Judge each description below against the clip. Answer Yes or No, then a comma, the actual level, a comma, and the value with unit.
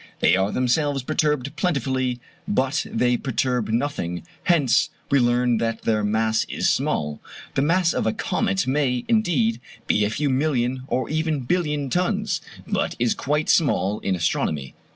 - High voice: No, low, 130 Hz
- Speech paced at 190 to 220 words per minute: No, average, 155 wpm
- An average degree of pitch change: Yes, average, 4.8 semitones